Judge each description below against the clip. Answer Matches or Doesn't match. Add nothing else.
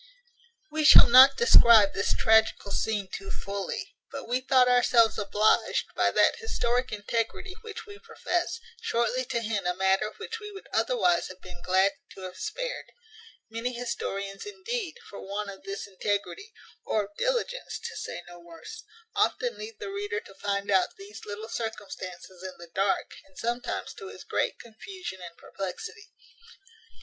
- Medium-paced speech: Matches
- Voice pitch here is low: Doesn't match